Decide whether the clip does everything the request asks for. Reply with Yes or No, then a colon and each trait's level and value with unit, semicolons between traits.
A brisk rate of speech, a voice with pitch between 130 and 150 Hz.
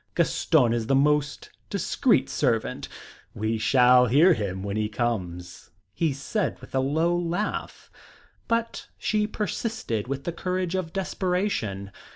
No: slow, 135 wpm; medium, 140 Hz